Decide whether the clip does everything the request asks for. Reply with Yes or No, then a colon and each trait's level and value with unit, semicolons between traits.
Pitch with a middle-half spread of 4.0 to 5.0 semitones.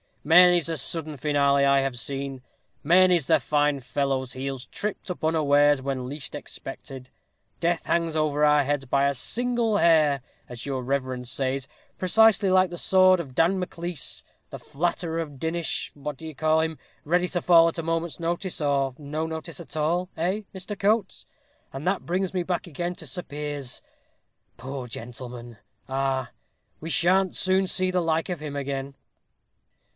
Yes: average, 4.3 semitones